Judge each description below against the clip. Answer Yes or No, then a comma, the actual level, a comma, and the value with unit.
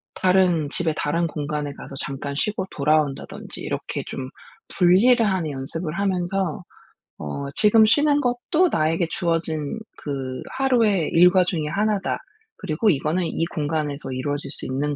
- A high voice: No, medium, 165 Hz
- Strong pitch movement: No, average, 4.8 semitones